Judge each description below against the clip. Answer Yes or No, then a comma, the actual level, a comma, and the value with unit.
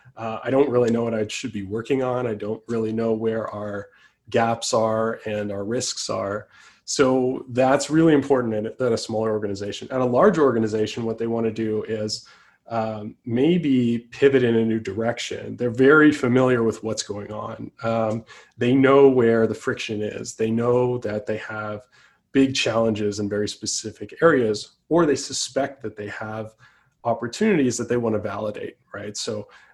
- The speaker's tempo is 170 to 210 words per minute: Yes, average, 190 wpm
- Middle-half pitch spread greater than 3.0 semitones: No, narrow, 2.6 semitones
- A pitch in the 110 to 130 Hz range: Yes, low, 115 Hz